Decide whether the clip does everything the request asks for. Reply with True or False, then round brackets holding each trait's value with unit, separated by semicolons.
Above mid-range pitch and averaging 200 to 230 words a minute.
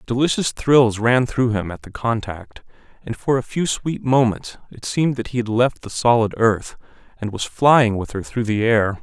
False (115 Hz; 205 wpm)